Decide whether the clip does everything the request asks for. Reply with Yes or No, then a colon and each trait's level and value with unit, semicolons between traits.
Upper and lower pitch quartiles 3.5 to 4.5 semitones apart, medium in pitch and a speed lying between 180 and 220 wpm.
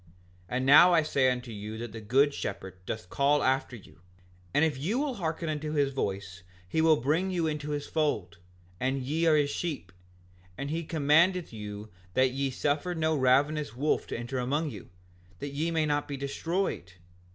Yes: average, 4.2 semitones; medium, 145 Hz; average, 190 wpm